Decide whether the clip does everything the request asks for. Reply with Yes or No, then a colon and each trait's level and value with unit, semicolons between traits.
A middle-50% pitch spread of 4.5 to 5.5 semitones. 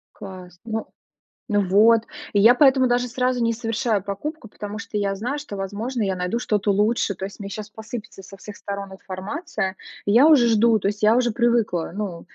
No: average, 3.2 semitones